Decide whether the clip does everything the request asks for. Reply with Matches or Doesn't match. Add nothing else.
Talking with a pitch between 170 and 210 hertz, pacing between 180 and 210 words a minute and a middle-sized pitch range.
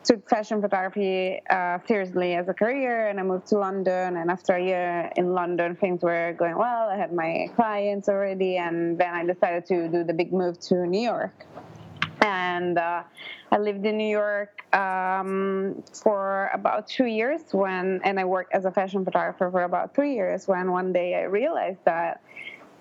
Doesn't match